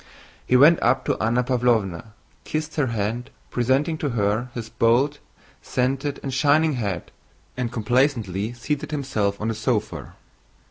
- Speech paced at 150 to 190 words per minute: No, average, 140 wpm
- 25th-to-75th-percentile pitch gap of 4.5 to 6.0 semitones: No, average, 3.9 semitones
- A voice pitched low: Yes, low, 125 Hz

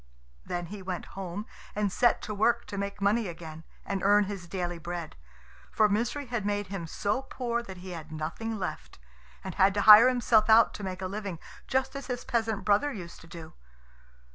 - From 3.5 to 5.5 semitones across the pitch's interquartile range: Yes, average, 3.8 semitones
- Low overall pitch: No, high, 200 Hz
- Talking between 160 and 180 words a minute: No, average, 195 wpm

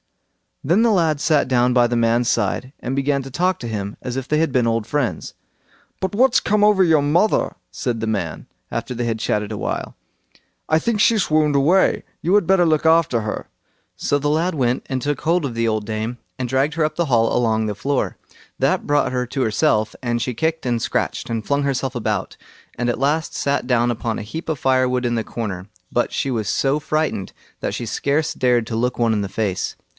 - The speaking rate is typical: No, fast, 220 wpm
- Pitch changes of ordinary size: Yes, average, 5.0 semitones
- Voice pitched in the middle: No, low, 130 Hz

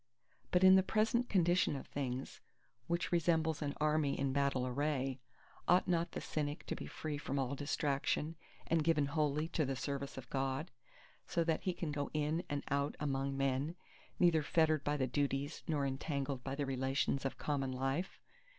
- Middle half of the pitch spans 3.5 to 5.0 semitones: No, average, 2.9 semitones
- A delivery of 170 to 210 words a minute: Yes, average, 180 wpm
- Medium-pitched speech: Yes, medium, 145 Hz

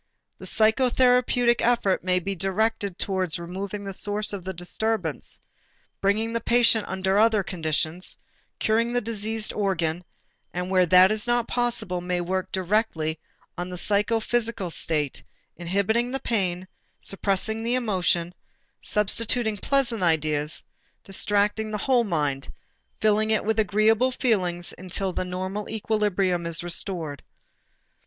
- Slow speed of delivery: Yes, slow, 130 wpm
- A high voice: Yes, high, 200 Hz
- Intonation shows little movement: No, average, 3.6 semitones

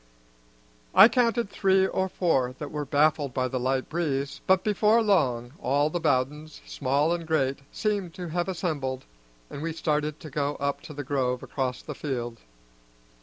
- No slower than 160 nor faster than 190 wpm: Yes, average, 170 wpm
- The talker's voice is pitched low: No, medium, 150 Hz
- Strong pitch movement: No, average, 4.7 semitones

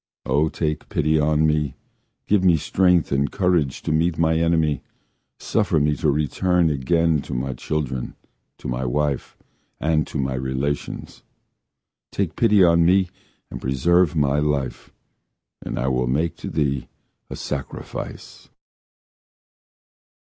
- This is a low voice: Yes, very low, 75 Hz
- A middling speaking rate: No, slow, 130 wpm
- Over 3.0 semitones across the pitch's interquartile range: Yes, average, 3.4 semitones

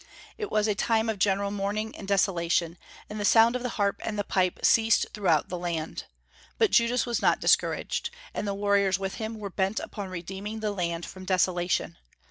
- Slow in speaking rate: No, average, 195 wpm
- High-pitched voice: Yes, high, 200 Hz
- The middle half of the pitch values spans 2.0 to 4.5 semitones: Yes, average, 2.9 semitones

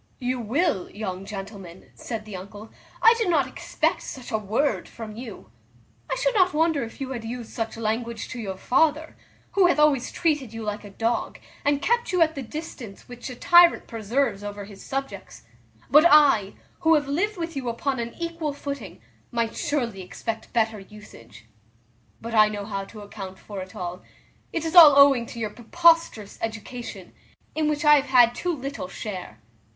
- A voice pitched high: Yes, high, 240 Hz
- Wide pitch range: Yes, wide, 5.9 semitones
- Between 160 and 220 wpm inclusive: Yes, average, 185 wpm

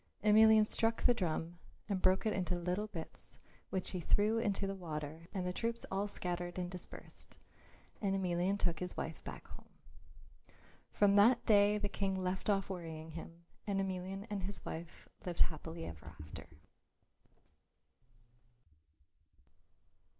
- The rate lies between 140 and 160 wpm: Yes, average, 145 wpm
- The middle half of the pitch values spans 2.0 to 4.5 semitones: Yes, average, 2.9 semitones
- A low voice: No, high, 190 Hz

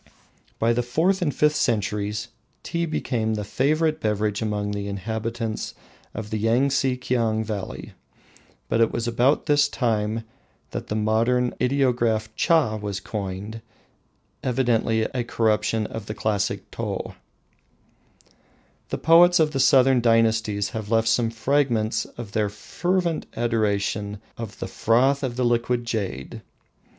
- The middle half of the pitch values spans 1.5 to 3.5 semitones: Yes, average, 3.0 semitones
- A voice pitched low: Yes, low, 115 Hz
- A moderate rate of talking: No, slow, 130 wpm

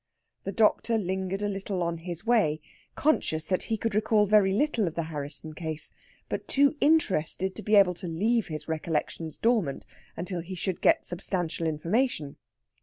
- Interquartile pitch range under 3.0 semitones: No, average, 4.8 semitones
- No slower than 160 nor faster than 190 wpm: Yes, average, 170 wpm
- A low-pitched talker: No, medium, 185 Hz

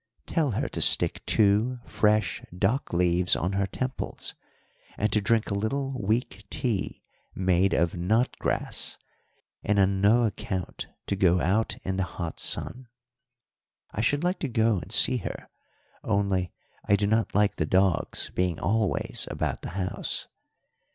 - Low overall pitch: Yes, low, 100 Hz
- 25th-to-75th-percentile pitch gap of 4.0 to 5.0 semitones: No, average, 3.3 semitones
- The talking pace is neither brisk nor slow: Yes, average, 150 wpm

